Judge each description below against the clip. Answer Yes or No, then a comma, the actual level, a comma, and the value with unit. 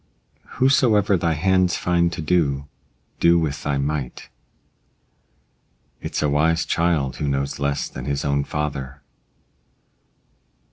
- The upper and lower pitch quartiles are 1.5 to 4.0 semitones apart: Yes, average, 3.5 semitones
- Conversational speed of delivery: No, slow, 120 wpm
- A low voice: Yes, very low, 75 Hz